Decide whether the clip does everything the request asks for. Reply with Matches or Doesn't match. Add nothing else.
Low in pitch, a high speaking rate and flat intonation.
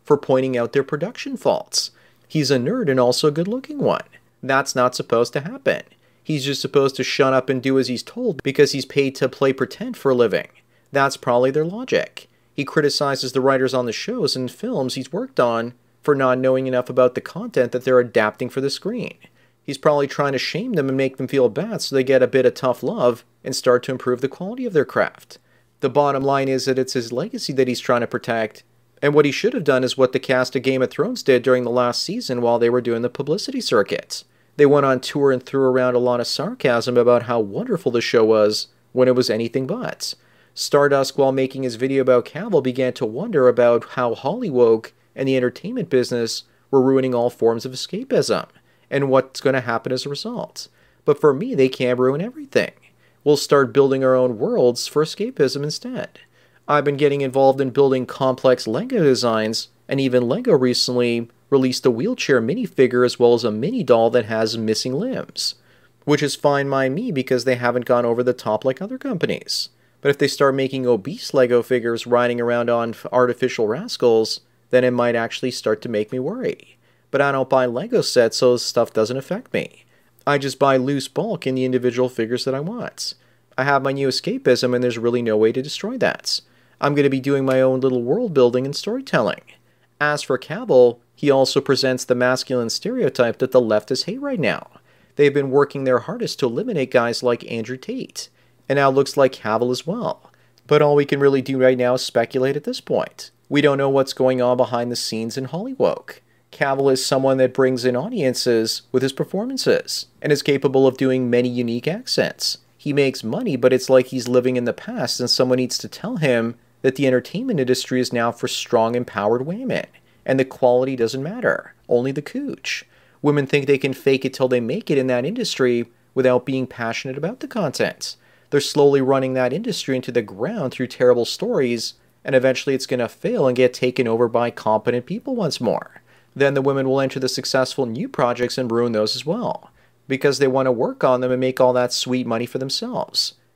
Matches